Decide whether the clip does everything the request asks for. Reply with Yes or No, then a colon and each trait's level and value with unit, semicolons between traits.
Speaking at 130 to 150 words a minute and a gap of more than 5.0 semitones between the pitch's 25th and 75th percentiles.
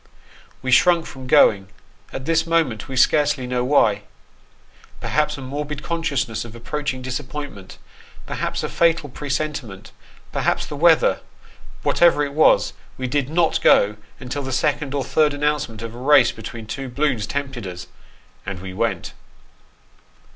No: average, 145 wpm; average, 3.8 semitones